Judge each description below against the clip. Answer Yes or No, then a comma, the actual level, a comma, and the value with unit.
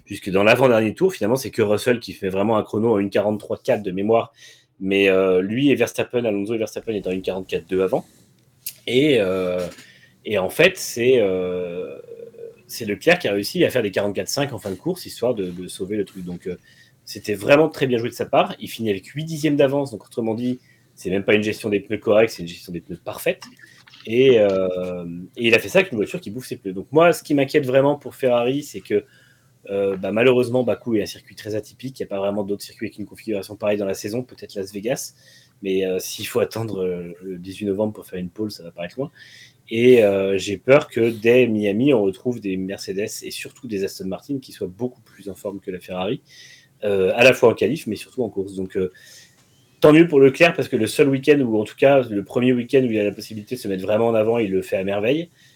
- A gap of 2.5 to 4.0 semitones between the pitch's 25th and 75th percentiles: No, average, 4.7 semitones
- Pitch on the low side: Yes, low, 105 Hz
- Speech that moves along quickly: Yes, fast, 240 wpm